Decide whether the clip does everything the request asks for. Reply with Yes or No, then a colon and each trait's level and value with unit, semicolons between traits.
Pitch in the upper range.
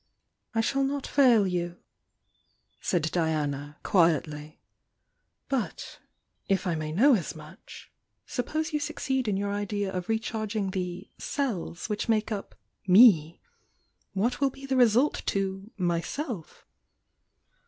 Yes: high, 200 Hz